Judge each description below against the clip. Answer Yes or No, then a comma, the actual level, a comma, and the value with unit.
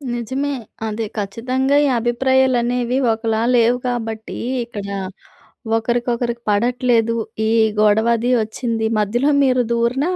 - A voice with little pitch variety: Yes, narrow, 2.1 semitones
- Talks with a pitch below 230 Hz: No, high, 235 Hz